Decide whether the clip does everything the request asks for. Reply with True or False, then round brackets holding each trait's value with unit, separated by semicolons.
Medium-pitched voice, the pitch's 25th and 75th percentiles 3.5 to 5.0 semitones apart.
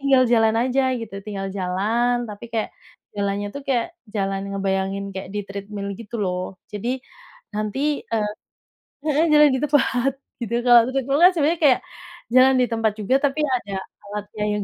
False (220 Hz; 4.6 semitones)